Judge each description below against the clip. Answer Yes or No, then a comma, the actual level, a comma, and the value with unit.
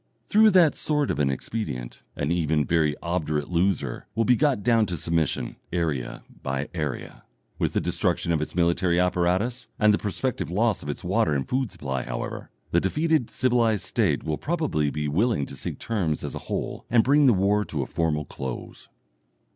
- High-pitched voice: No, very low, 90 Hz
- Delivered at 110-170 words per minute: No, average, 185 wpm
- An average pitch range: No, wide, 7.3 semitones